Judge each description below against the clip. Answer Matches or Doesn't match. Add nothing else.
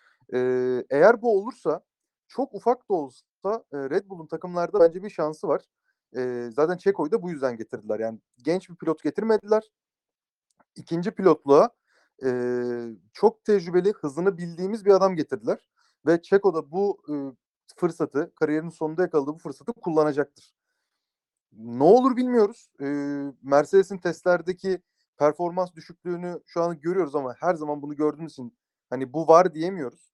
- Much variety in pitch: Doesn't match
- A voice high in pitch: Doesn't match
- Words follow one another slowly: Doesn't match